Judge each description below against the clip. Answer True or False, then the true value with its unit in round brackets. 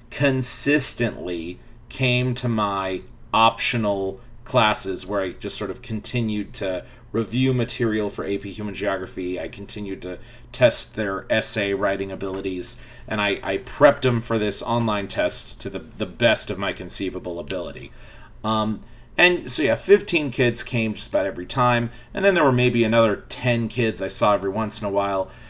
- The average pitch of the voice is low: True (110 Hz)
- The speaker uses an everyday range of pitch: True (3.8 semitones)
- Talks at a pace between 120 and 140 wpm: False (165 wpm)